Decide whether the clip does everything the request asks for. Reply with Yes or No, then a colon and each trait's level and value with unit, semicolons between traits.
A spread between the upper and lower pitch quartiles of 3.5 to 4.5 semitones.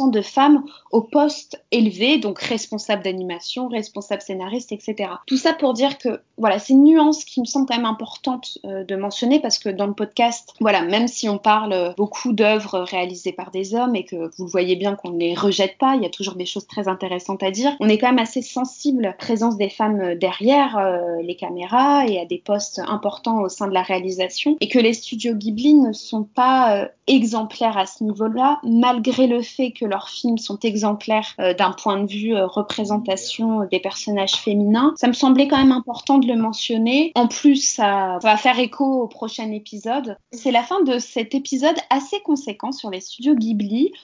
Yes: average, 4.1 semitones